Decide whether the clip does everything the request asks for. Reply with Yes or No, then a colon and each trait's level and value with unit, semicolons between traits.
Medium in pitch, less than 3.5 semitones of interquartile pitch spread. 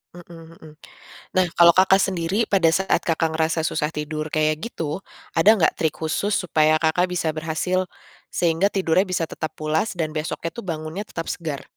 Yes: medium, 165 Hz; average, 2.7 semitones